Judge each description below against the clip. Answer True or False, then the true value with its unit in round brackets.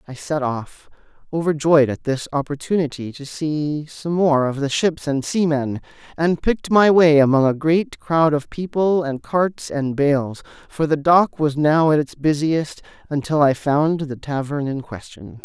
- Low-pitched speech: False (150 Hz)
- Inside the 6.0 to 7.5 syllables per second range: False (4.2 syllables/s)